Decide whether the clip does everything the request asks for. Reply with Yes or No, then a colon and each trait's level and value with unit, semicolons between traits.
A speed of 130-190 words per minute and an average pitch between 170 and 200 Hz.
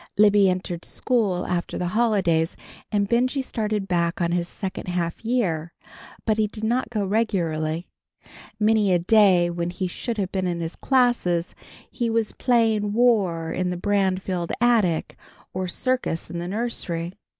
Yes: average, 155 wpm; high, 190 Hz